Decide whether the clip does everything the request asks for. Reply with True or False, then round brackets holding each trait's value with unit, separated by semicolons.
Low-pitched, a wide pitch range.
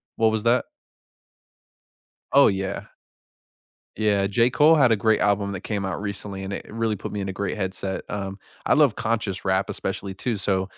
False (100 Hz; 2.5 semitones)